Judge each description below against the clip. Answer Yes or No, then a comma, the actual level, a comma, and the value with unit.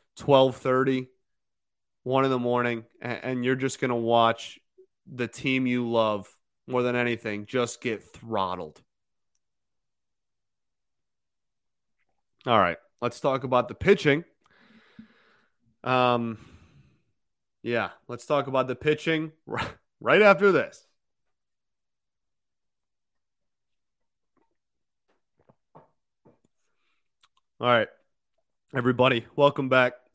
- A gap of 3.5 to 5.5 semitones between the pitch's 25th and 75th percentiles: No, average, 2.9 semitones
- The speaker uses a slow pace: Yes, slow, 85 wpm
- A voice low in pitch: Yes, low, 130 Hz